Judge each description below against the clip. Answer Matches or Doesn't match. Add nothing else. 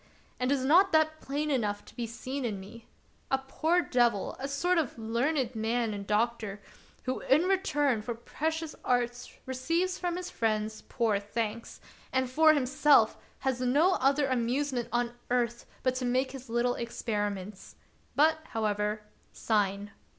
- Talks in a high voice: Matches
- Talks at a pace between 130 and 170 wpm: Matches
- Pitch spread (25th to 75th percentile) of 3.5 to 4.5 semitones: Matches